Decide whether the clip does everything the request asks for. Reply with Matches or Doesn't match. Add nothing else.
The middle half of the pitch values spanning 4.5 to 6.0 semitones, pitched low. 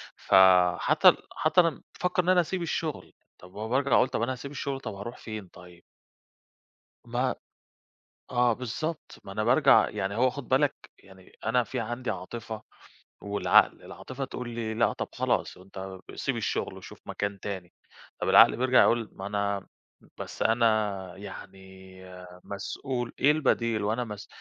Matches